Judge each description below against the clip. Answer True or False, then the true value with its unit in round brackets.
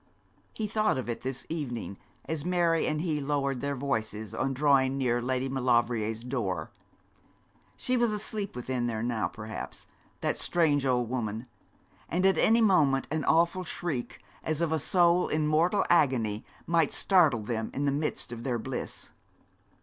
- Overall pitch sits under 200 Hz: True (135 Hz)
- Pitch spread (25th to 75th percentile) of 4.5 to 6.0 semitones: True (5.5 semitones)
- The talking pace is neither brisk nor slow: True (160 wpm)